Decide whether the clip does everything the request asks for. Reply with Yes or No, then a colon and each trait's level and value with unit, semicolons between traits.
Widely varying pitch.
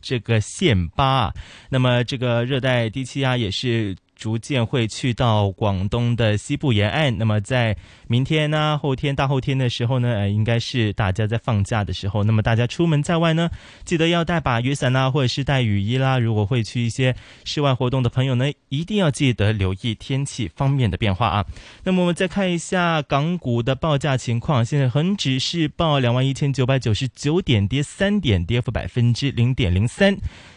No: average, 4.1 semitones